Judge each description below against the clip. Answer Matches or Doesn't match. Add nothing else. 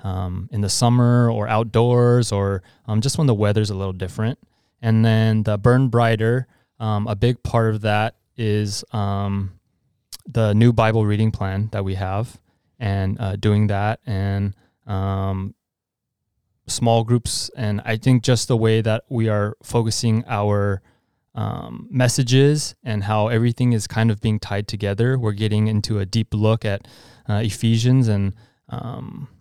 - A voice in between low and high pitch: Doesn't match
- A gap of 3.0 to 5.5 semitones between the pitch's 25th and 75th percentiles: Doesn't match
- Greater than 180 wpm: Doesn't match